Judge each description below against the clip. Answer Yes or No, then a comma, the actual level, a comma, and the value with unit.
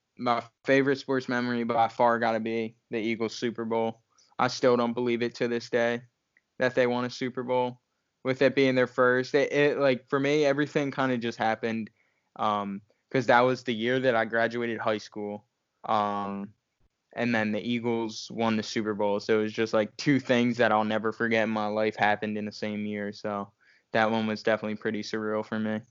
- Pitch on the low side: Yes, low, 115 Hz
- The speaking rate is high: Yes, fast, 210 wpm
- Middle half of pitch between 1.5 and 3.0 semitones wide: Yes, narrow, 2.4 semitones